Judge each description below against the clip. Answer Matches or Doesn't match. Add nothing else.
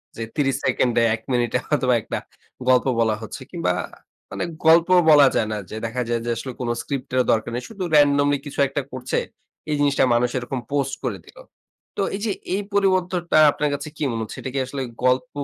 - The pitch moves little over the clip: Doesn't match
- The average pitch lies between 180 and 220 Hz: Doesn't match